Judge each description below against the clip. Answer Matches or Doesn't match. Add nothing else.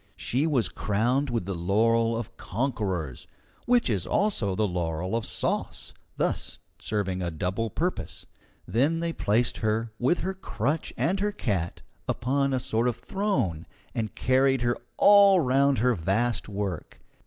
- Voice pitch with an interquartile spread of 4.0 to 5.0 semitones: Doesn't match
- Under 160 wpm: Matches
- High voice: Doesn't match